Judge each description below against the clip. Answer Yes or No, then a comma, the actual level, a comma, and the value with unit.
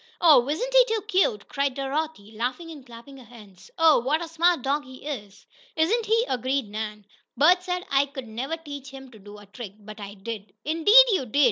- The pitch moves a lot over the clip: Yes, wide, 6.6 semitones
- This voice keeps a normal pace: No, fast, 210 wpm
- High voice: Yes, very high, 275 Hz